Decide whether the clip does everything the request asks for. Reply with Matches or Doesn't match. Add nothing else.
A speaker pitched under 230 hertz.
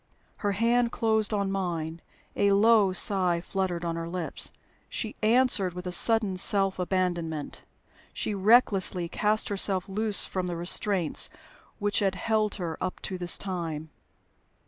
Matches